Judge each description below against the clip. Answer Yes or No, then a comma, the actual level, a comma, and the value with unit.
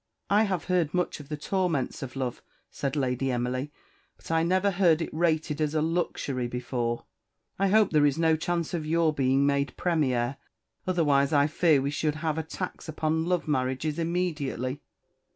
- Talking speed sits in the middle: Yes, average, 175 wpm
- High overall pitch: No, medium, 155 Hz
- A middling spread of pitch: Yes, average, 3.7 semitones